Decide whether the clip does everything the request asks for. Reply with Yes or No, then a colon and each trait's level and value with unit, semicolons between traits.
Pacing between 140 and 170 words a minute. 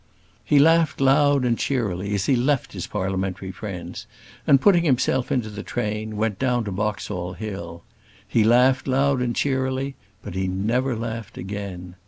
Yes: average, 160 wpm